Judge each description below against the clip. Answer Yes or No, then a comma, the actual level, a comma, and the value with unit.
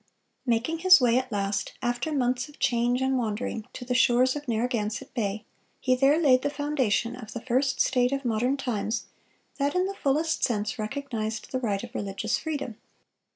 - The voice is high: Yes, very high, 250 Hz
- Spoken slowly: No, average, 180 wpm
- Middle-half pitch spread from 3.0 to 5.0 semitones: Yes, average, 3.3 semitones